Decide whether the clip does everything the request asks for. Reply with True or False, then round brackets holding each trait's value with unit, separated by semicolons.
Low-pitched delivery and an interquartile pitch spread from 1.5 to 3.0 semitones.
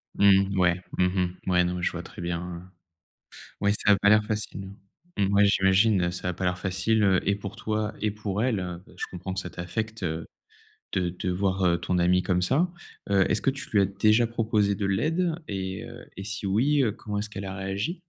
True (95 Hz; 2.6 semitones)